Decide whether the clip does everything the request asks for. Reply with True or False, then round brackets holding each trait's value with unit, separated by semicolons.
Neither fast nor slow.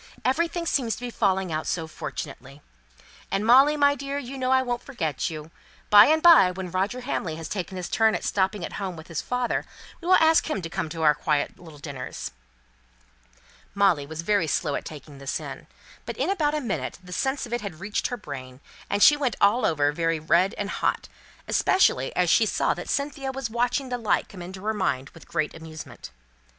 False (210 wpm)